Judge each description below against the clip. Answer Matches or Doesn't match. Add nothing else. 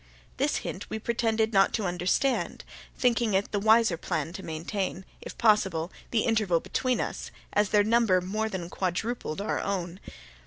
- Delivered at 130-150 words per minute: Doesn't match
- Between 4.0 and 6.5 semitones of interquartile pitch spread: Doesn't match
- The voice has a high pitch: Matches